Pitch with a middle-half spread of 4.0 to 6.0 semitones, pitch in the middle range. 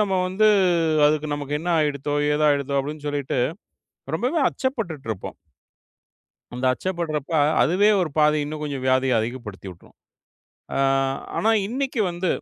Yes: average, 4.8 semitones; medium, 150 Hz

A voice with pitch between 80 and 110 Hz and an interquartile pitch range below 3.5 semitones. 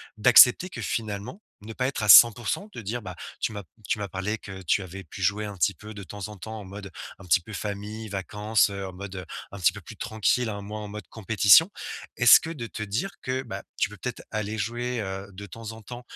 Yes: low, 105 Hz; narrow, 2.5 semitones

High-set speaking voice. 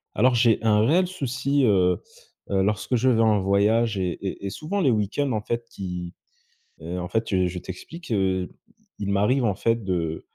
No: low, 105 Hz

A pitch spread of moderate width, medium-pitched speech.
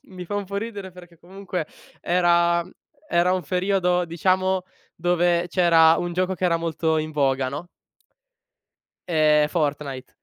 No: narrow, 2.3 semitones; medium, 175 Hz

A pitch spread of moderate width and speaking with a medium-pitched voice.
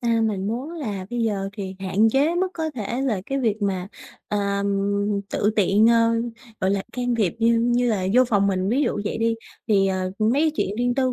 No: average, 3.7 semitones; high, 220 Hz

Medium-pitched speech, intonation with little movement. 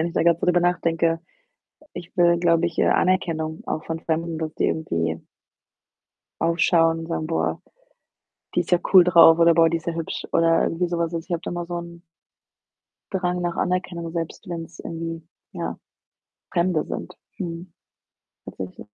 Yes: medium, 170 Hz; narrow, 1.1 semitones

